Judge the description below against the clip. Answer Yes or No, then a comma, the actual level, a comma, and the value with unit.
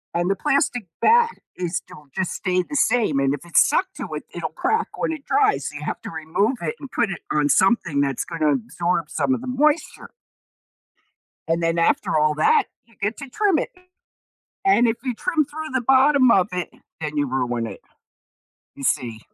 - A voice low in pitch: No, high, 190 Hz